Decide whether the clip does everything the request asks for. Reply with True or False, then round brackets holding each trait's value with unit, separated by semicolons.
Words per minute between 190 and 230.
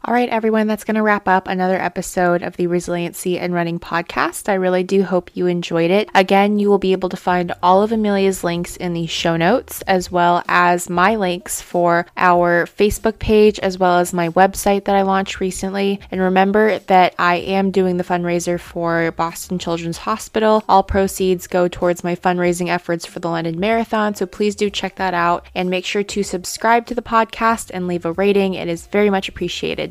True (205 wpm)